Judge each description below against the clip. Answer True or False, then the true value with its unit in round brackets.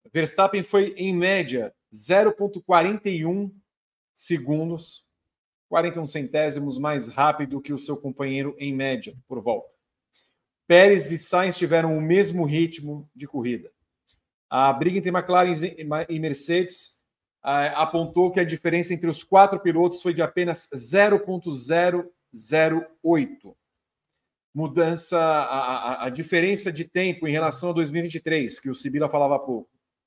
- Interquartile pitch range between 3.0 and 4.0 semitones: True (3.5 semitones)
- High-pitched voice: False (165 Hz)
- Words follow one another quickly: False (125 wpm)